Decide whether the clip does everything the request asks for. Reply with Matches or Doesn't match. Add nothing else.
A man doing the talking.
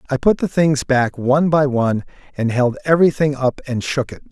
Matches